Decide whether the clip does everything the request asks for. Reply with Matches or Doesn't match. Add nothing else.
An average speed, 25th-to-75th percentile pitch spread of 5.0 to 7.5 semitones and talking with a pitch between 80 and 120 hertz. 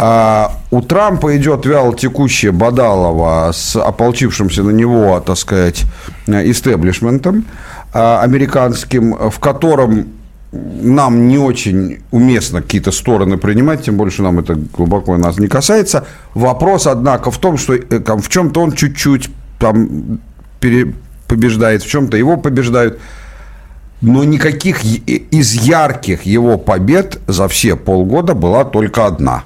Matches